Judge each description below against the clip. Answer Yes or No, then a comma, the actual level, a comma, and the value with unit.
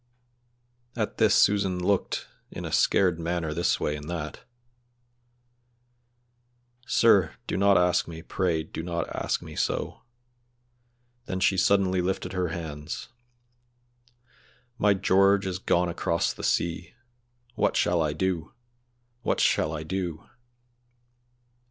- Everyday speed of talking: No, slow, 120 wpm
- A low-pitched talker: Yes, very low, 90 Hz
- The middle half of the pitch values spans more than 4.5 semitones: No, narrow, 2.6 semitones